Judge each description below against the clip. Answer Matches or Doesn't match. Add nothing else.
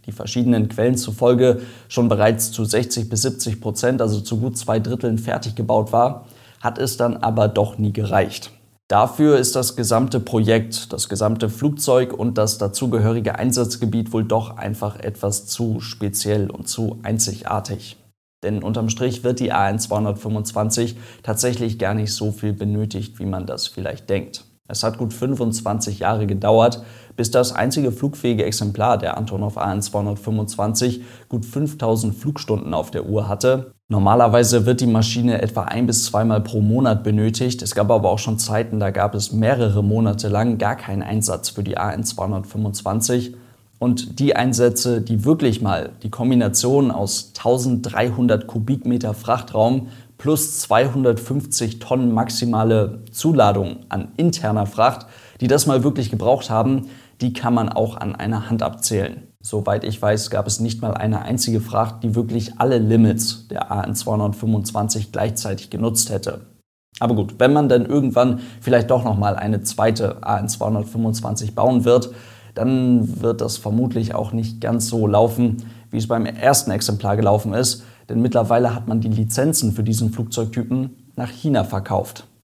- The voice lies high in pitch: Doesn't match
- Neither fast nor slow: Matches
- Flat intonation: Matches